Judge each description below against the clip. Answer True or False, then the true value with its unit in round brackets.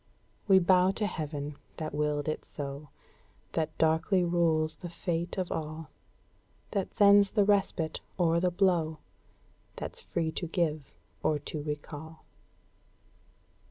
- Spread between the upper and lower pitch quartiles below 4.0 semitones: True (2.8 semitones)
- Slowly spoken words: True (125 wpm)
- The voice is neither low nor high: True (160 Hz)